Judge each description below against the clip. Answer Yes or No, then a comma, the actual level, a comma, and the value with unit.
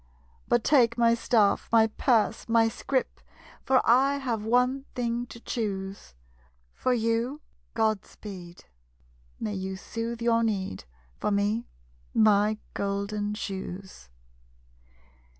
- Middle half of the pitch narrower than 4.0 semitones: Yes, average, 2.7 semitones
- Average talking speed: No, slow, 110 wpm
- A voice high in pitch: Yes, high, 225 Hz